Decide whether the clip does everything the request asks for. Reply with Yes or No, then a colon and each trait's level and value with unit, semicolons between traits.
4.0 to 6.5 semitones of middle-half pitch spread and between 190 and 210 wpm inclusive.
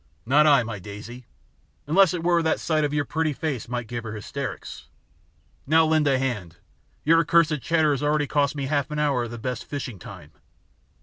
Yes: average, 4.3 semitones; average, 200 wpm